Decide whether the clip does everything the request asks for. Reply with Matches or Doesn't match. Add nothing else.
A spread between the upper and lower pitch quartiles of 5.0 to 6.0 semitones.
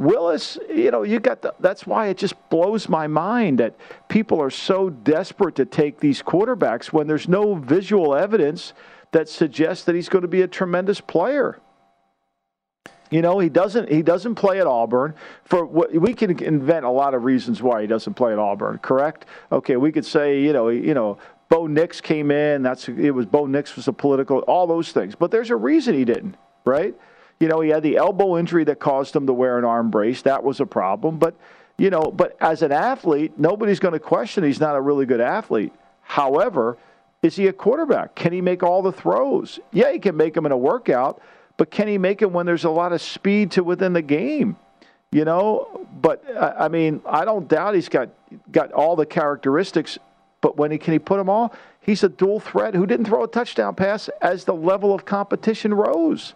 Matches